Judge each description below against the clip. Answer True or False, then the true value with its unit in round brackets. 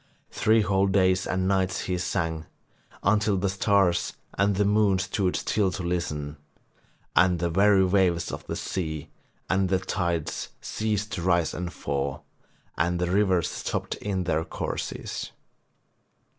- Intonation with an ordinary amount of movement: False (2.3 semitones)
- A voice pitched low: True (95 Hz)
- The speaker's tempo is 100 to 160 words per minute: True (145 wpm)